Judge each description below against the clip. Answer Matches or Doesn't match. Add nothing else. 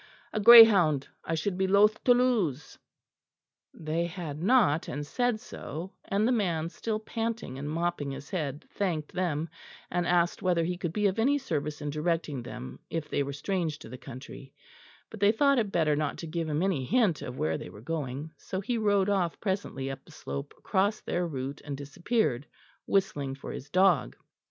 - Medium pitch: Matches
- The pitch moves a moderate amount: Doesn't match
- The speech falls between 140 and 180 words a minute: Doesn't match